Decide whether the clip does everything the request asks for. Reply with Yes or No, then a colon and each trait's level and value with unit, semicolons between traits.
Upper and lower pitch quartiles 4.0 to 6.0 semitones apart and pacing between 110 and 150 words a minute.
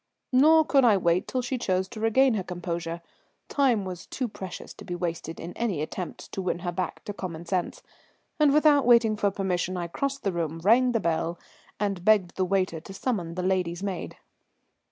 No: average, 5.1 semitones; average, 195 wpm